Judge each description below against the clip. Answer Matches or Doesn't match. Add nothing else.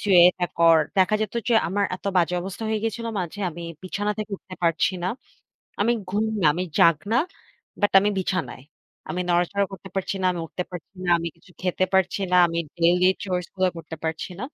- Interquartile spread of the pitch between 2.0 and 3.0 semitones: Matches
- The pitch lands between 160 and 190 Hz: Matches